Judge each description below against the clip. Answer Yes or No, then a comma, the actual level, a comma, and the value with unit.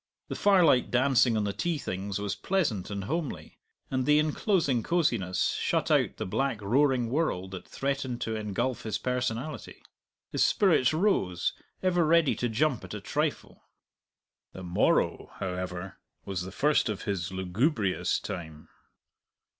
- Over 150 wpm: No, average, 145 wpm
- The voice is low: Yes, low, 120 Hz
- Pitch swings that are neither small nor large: No, wide, 7.4 semitones